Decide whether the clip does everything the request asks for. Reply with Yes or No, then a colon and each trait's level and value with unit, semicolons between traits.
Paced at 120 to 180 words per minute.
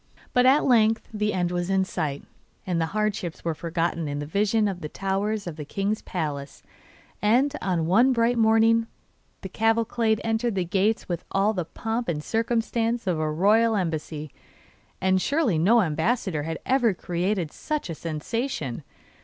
Yes: average, 160 wpm